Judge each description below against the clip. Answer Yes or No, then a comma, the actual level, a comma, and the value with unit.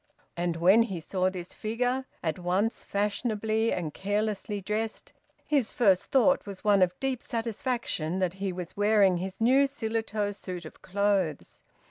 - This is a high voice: Yes, high, 205 Hz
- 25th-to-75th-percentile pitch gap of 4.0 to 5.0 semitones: No, average, 3.5 semitones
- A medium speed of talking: Yes, average, 150 wpm